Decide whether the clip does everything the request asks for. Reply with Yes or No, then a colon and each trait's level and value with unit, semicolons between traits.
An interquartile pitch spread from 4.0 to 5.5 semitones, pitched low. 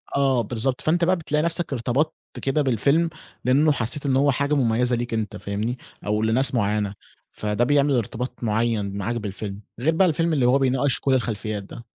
Yes: average, 4.4 semitones; low, 125 Hz